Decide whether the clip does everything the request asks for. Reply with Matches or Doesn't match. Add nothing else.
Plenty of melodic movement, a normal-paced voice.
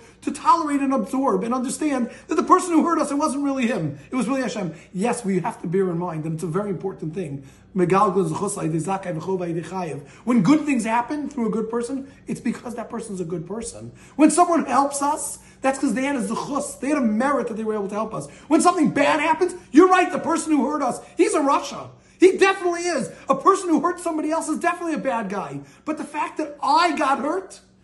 Doesn't match